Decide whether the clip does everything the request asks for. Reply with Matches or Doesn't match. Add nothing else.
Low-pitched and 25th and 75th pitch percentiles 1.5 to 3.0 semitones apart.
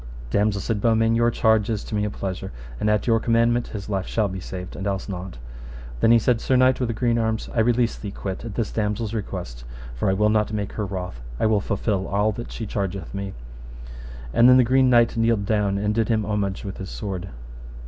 Matches